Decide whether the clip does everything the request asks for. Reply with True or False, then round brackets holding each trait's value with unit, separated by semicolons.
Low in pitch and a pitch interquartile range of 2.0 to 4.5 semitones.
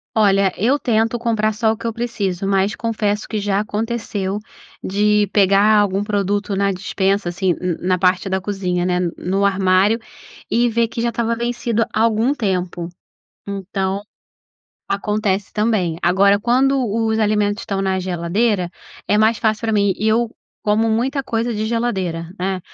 False (205 Hz; 2.8 semitones)